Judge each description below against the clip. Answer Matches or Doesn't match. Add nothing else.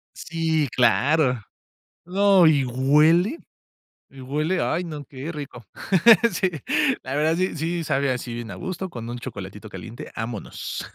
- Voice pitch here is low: Doesn't match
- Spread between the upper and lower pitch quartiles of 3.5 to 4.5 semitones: Doesn't match